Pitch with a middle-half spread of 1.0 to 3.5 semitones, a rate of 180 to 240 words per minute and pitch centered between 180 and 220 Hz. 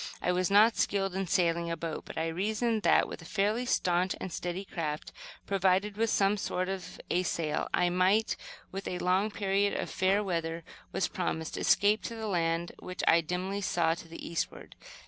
Yes: average, 2.9 semitones; average, 190 wpm; medium, 185 Hz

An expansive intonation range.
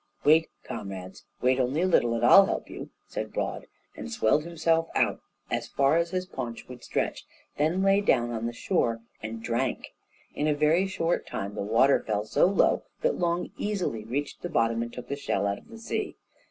Yes: wide, 6.8 semitones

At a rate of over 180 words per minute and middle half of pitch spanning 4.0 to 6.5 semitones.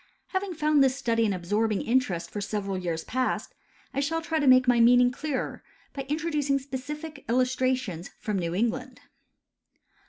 No: average, 155 wpm; average, 5.1 semitones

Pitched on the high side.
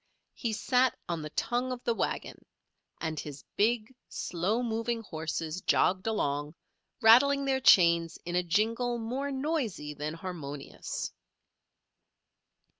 Yes: high, 215 Hz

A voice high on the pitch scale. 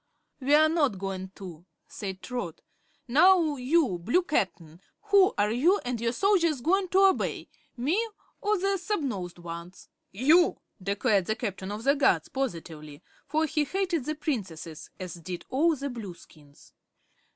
Yes: very high, 250 Hz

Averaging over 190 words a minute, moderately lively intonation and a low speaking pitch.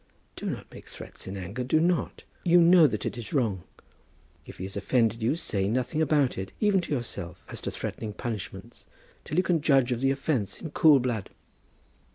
No: average, 200 wpm; wide, 6.8 semitones; low, 125 Hz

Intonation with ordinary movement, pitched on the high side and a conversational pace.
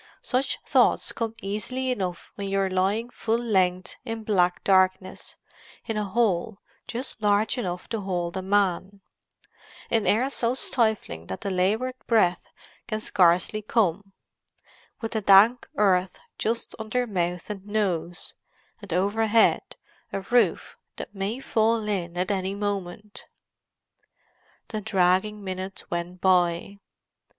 No: average, 3.0 semitones; high, 200 Hz; slow, 130 wpm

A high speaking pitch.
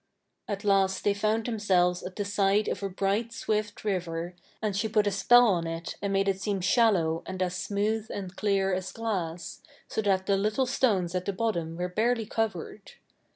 Yes: high, 200 Hz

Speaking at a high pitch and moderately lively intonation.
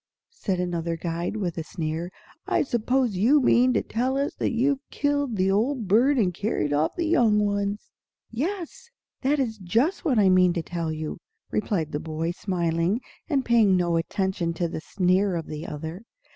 No: high, 195 Hz; wide, 6.6 semitones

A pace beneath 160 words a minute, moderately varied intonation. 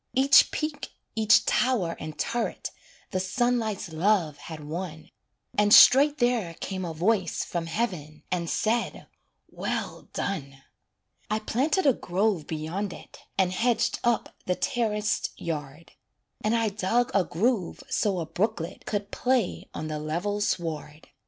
No: average, 140 wpm; wide, 5.7 semitones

